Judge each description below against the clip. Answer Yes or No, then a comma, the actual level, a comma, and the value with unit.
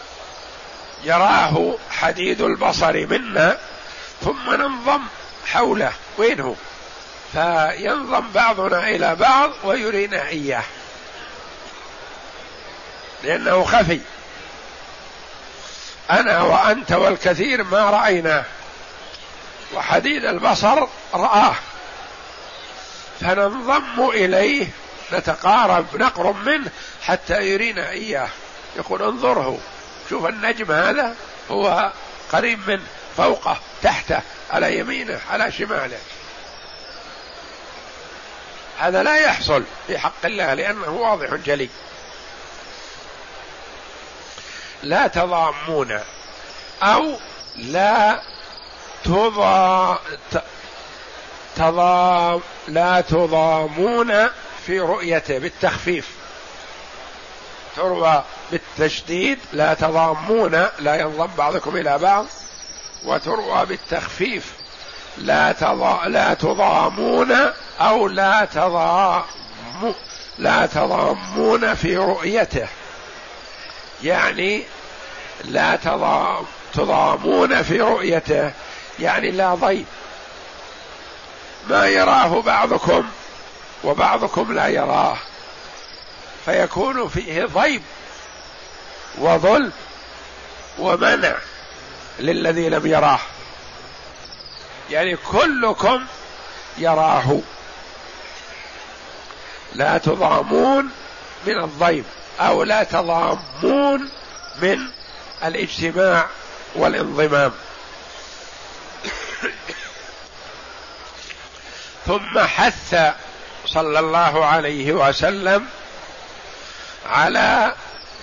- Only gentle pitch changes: No, average, 4.6 semitones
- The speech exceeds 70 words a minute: No, slow, 65 wpm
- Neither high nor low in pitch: Yes, medium, 180 Hz